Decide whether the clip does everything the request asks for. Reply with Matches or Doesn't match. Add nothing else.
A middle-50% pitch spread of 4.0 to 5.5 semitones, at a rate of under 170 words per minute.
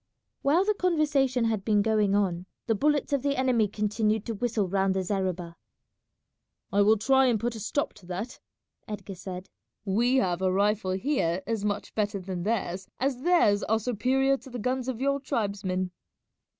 Doesn't match